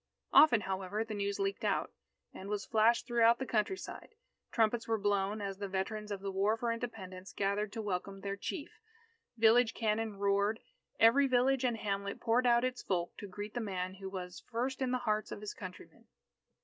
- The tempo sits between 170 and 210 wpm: Yes, average, 190 wpm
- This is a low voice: No, high, 210 Hz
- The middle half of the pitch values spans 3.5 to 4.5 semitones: No, average, 3.0 semitones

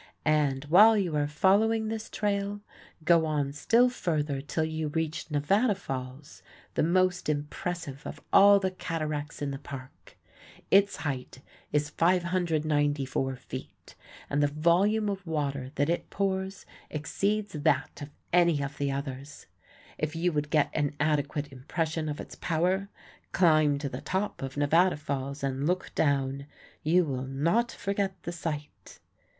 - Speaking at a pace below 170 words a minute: Yes, average, 145 wpm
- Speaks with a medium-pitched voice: Yes, medium, 155 Hz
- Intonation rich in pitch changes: No, average, 4.3 semitones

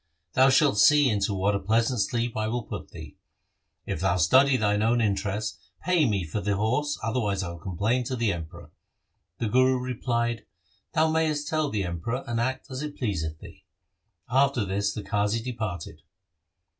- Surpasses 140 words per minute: Yes, average, 180 wpm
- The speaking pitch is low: Yes, low, 115 Hz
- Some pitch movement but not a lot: Yes, average, 4.2 semitones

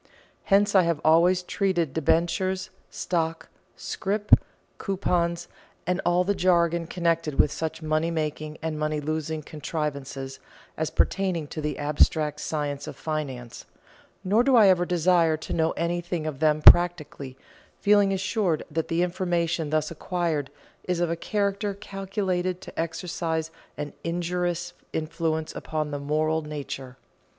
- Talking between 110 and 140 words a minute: Yes, slow, 135 wpm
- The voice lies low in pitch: No, medium, 165 Hz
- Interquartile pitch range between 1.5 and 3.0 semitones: Yes, average, 2.7 semitones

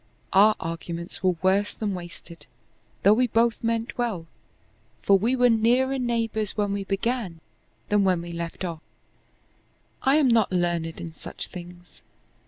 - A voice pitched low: No, high, 200 Hz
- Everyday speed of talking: Yes, average, 150 wpm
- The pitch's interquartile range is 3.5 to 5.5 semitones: Yes, average, 4.9 semitones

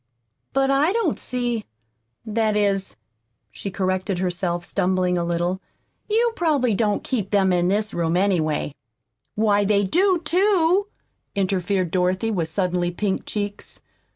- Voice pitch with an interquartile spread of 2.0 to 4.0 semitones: No, average, 5.0 semitones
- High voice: Yes, high, 200 Hz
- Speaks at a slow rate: Yes, slow, 130 wpm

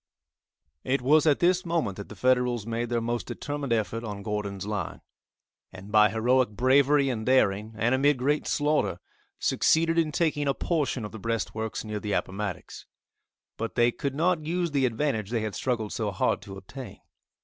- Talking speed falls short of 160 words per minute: No, average, 175 wpm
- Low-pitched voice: Yes, low, 120 Hz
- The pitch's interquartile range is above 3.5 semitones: Yes, average, 5.1 semitones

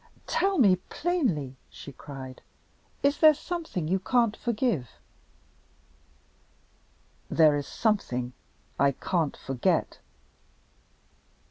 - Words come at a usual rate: No, slow, 90 wpm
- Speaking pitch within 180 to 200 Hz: Yes, medium, 185 Hz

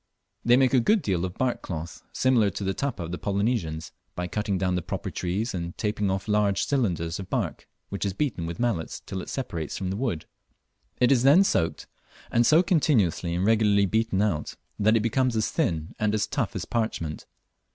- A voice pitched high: No, low, 105 Hz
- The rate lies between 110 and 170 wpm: No, fast, 205 wpm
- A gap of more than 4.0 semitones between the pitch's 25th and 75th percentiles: Yes, average, 5.2 semitones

